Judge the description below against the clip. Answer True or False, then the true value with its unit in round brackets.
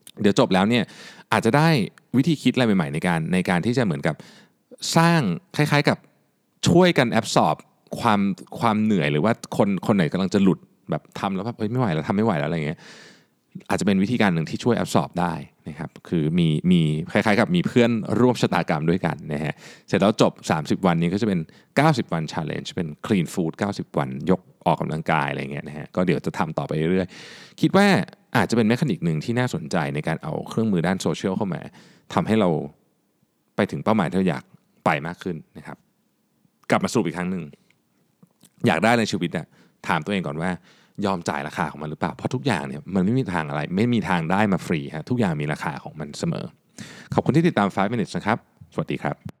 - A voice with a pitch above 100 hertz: True (115 Hz)